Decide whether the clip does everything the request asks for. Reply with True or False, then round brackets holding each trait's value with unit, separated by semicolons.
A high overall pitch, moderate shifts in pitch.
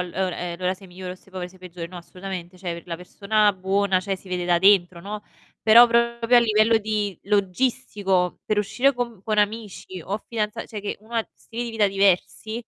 True (200 Hz; 3.0 semitones)